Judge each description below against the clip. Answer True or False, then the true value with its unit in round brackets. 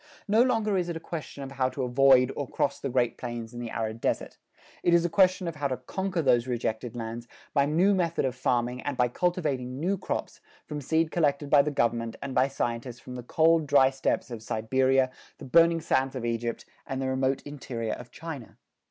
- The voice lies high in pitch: False (135 Hz)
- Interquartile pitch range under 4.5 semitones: False (4.8 semitones)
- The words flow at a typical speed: False (215 wpm)